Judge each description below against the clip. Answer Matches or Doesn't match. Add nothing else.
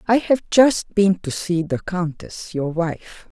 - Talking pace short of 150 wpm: Doesn't match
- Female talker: Matches